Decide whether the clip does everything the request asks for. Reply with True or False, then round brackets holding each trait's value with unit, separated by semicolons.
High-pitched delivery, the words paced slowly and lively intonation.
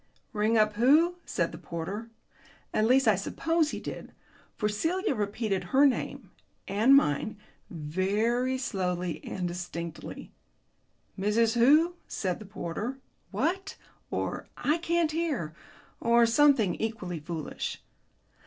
True (220 Hz; 120 wpm; 6.7 semitones)